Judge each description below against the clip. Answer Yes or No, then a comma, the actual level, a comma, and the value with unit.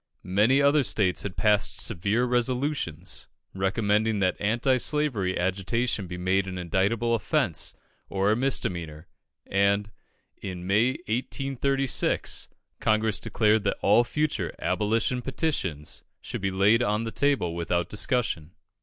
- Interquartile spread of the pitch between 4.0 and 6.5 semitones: Yes, average, 4.5 semitones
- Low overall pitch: Yes, low, 105 Hz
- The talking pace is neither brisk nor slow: No, slow, 125 wpm